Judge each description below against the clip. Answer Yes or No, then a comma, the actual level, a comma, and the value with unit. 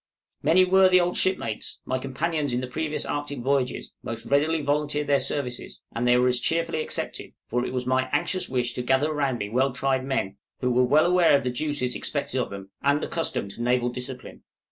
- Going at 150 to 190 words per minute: No, average, 200 wpm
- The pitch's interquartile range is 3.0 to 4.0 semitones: Yes, average, 3.3 semitones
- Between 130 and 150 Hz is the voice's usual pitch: Yes, low, 135 Hz